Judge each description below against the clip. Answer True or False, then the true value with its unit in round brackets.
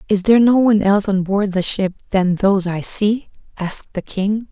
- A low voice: False (200 Hz)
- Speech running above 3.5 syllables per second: True (5.4 syllables/s)